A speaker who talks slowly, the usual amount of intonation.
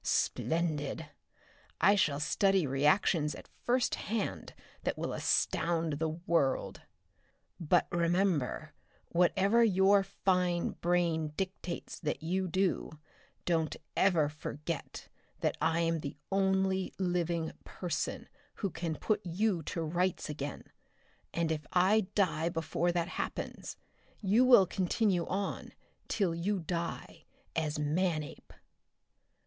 Yes: slow, 115 wpm; average, 3.1 semitones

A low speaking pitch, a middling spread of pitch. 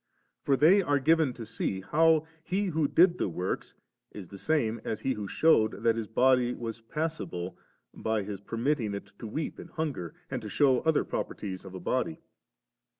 No: low, 120 Hz; wide, 6.8 semitones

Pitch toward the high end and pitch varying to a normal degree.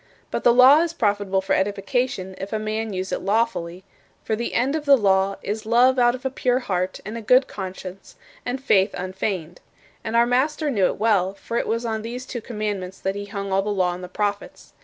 Yes: high, 215 Hz; average, 4.2 semitones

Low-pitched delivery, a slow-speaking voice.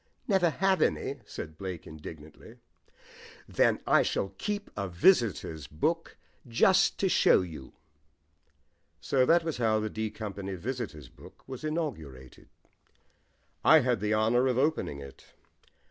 Yes: low, 110 Hz; slow, 130 wpm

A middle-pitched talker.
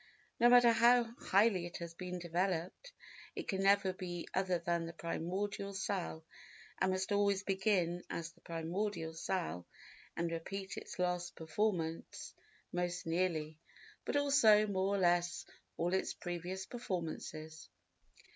Yes: medium, 180 Hz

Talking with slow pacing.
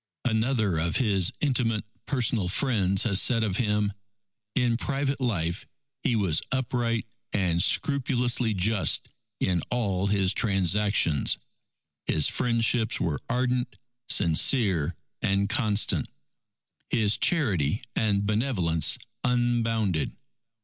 Yes: slow, 100 wpm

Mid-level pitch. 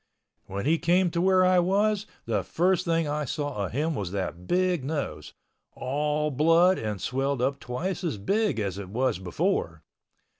Yes: medium, 150 Hz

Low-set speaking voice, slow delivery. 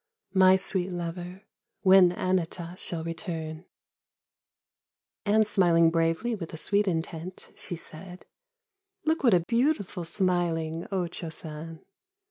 No: medium, 180 Hz; slow, 125 wpm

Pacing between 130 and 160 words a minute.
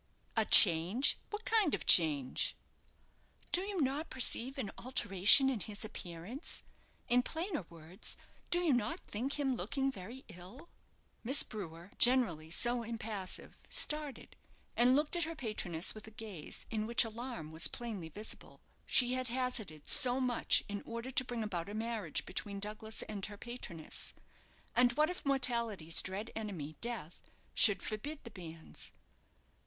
Yes: average, 150 wpm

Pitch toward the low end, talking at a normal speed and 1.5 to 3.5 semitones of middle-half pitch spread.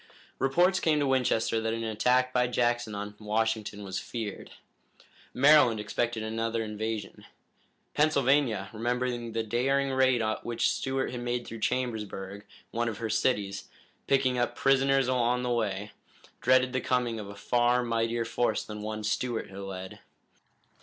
Yes: low, 120 Hz; average, 150 wpm; average, 2.7 semitones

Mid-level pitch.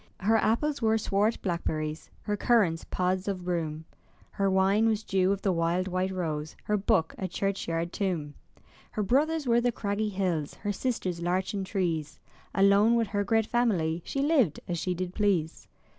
No: high, 195 Hz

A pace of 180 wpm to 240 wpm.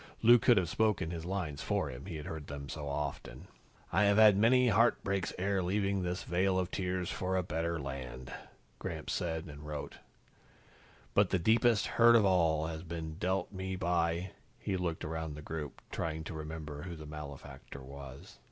Yes: average, 185 wpm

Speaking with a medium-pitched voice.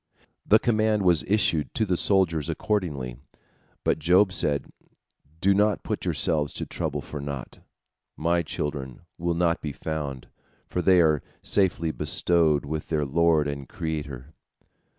No: very low, 80 Hz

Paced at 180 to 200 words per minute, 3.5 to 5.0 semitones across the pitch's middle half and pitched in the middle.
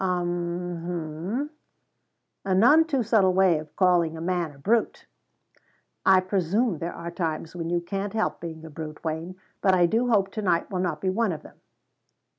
No: average, 185 wpm; average, 2.8 semitones; medium, 180 Hz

